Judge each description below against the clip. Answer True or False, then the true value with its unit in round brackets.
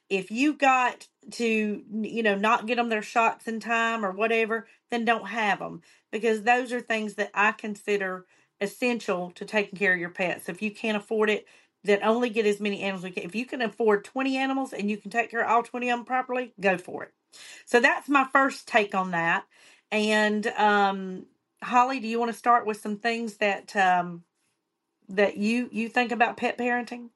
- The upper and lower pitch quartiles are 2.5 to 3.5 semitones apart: True (2.9 semitones)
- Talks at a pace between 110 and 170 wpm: False (205 wpm)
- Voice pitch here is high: True (220 Hz)